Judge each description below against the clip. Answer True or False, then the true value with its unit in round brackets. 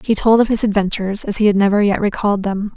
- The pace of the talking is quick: True (260 wpm)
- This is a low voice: False (205 Hz)